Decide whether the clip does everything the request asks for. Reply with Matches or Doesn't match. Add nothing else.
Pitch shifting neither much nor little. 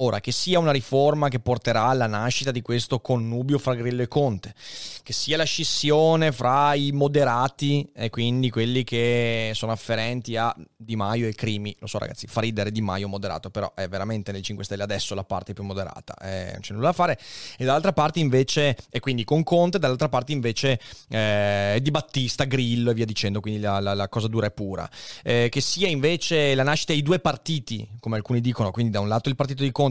Matches